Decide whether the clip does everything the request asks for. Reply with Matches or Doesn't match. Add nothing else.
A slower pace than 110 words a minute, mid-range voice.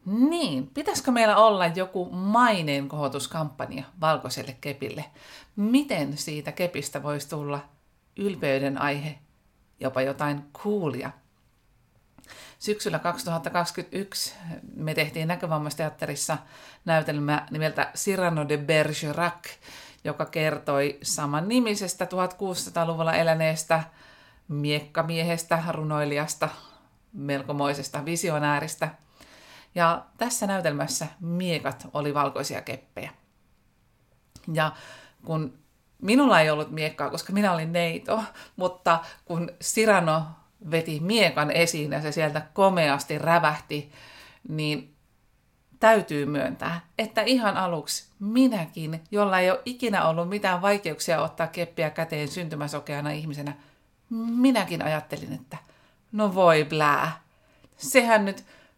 Matches